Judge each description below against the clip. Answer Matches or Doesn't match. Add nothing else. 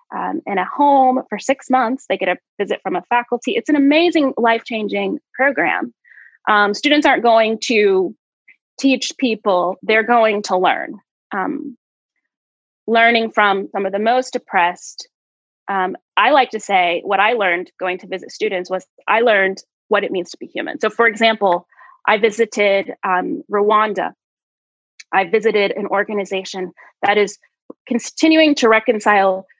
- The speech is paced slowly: Doesn't match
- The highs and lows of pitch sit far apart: Doesn't match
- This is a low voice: Doesn't match